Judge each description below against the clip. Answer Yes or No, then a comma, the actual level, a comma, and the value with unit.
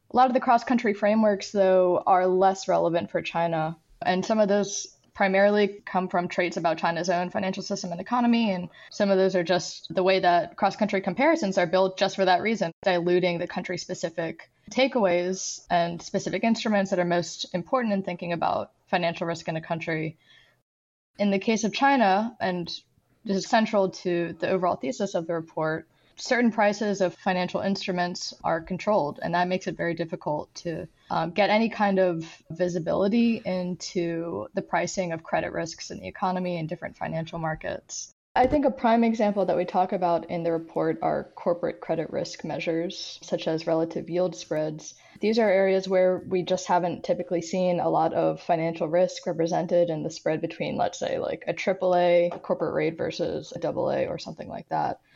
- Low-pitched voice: No, medium, 180 Hz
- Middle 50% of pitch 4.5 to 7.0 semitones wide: No, narrow, 2.6 semitones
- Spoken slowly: No, average, 185 wpm